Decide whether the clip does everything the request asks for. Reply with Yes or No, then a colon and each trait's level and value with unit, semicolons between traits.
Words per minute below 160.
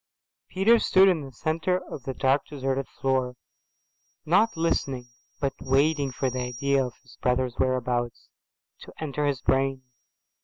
Yes: average, 145 wpm